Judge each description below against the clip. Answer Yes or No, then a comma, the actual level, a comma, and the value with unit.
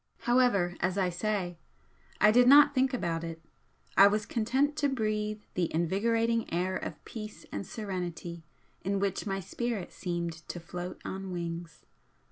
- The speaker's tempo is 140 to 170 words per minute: Yes, average, 150 wpm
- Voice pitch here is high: Yes, high, 195 Hz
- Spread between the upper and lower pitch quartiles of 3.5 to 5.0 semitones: Yes, average, 4.4 semitones